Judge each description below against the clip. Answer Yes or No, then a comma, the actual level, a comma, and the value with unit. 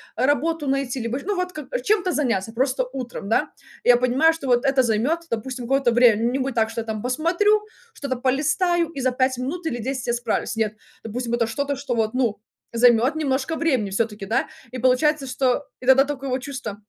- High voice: Yes, very high, 260 Hz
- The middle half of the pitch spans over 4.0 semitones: No, average, 3.1 semitones